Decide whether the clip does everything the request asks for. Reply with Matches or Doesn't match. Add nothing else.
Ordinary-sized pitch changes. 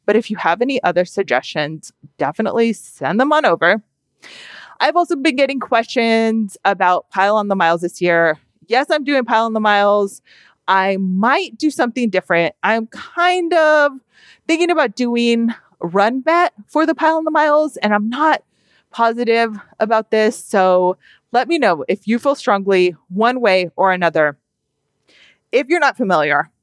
Doesn't match